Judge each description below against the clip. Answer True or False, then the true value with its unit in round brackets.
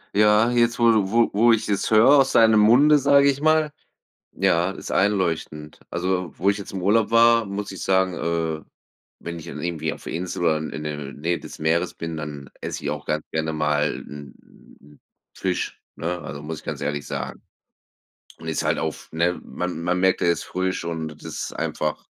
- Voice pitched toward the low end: True (90 Hz)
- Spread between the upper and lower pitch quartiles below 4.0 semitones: False (5.3 semitones)